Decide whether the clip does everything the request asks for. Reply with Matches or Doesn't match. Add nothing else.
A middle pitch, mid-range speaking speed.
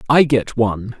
Doesn't match